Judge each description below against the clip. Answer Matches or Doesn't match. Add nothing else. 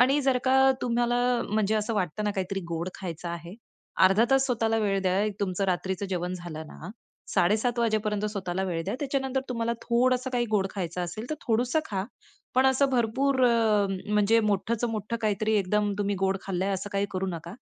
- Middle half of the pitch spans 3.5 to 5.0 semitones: Matches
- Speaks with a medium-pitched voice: Doesn't match